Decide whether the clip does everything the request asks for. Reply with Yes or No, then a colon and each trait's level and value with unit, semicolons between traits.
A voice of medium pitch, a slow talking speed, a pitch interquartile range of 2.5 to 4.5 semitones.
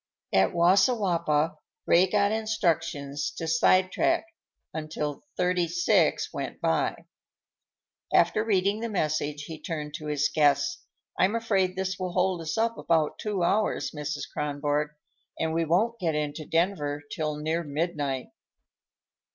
Yes: medium, 165 Hz; slow, 130 wpm; average, 4.2 semitones